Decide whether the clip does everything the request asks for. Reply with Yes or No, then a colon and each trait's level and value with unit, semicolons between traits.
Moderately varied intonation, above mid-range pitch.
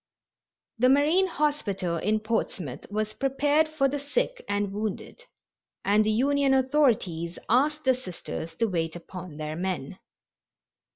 No: wide, 7.6 semitones; high, 220 Hz